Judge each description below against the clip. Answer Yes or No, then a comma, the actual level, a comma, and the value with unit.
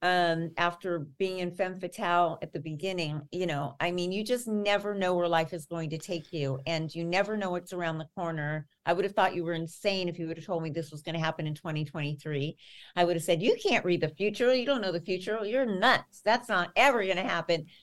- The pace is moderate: No, fast, 250 wpm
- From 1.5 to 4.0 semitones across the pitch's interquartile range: Yes, average, 2.8 semitones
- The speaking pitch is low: No, medium, 175 Hz